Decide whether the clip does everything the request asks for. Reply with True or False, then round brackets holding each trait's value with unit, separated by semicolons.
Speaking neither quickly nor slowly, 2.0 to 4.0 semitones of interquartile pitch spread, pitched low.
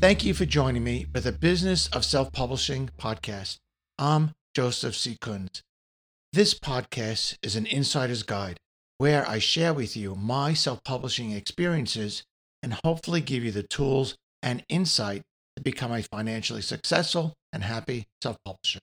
False (155 wpm; 5.1 semitones; 125 Hz)